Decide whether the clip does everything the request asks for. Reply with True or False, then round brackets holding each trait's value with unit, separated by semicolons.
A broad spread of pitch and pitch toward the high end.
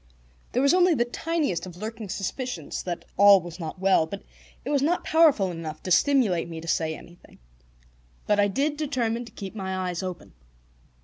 True (7.1 semitones; 200 Hz)